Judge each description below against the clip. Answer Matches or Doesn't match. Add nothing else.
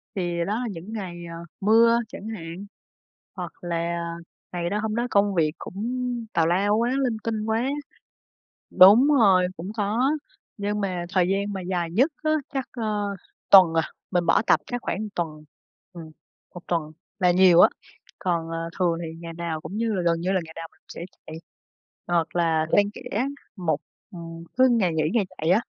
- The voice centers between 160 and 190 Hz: Matches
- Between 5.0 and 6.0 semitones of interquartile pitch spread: Doesn't match